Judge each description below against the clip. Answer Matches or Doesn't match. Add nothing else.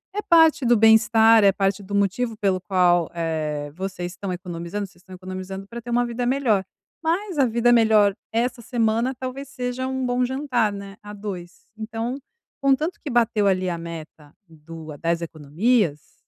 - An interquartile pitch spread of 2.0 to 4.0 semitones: Doesn't match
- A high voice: Matches